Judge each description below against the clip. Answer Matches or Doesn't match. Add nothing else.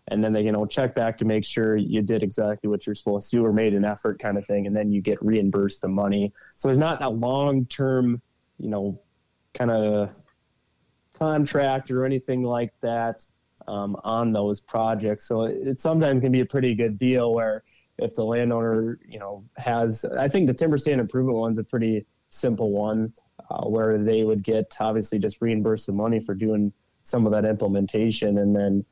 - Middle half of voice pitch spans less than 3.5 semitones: Matches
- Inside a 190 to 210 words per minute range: Matches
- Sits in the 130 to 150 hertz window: Doesn't match